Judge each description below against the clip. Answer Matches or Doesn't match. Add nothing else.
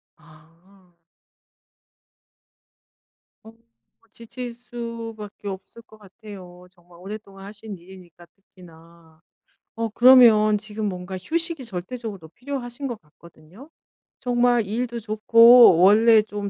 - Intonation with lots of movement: Doesn't match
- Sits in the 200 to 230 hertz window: Matches